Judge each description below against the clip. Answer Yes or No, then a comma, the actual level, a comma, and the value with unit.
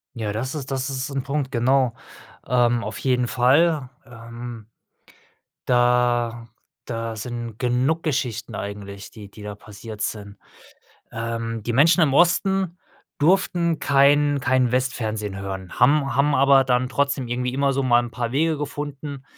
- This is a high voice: No, low, 125 Hz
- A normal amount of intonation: Yes, average, 3.3 semitones